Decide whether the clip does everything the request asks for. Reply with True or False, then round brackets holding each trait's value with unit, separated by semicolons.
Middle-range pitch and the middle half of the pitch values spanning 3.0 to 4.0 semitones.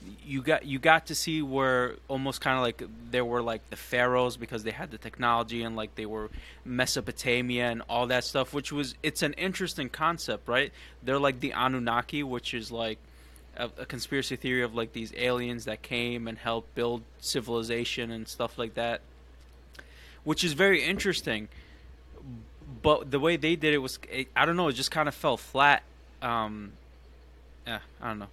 False (120 Hz; 3.5 semitones)